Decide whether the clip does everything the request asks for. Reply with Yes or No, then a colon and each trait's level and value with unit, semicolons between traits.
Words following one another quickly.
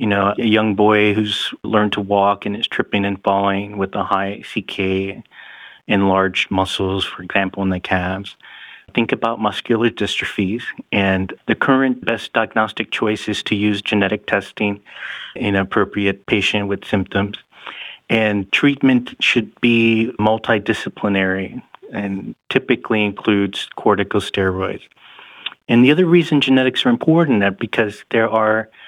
No: slow, 135 wpm